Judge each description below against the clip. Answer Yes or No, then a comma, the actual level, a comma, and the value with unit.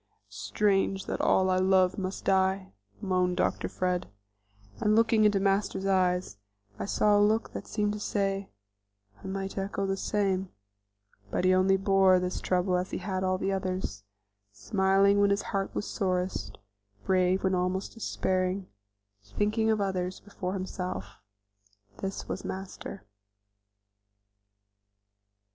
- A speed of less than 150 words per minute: Yes, slow, 135 wpm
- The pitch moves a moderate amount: No, narrow, 1.2 semitones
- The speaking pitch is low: No, high, 190 Hz